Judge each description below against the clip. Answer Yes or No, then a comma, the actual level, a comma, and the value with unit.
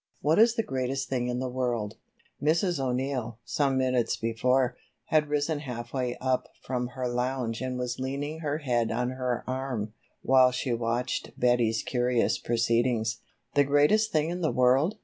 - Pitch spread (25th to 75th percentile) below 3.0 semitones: Yes, narrow, 2.5 semitones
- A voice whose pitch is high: No, low, 130 Hz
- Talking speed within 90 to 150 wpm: No, average, 165 wpm